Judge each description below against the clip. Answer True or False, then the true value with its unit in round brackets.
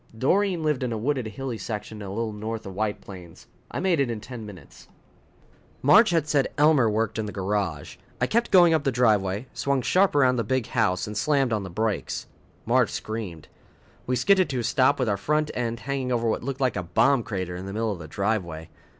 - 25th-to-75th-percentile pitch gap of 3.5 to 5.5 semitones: True (5.0 semitones)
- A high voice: False (115 Hz)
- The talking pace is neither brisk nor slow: False (220 wpm)